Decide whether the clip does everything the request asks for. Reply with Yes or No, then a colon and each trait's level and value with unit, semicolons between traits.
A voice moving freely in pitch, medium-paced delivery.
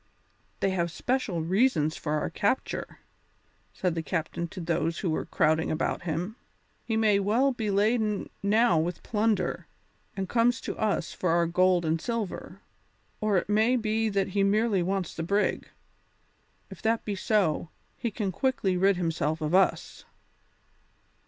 No: average, 4.3 semitones; average, 155 wpm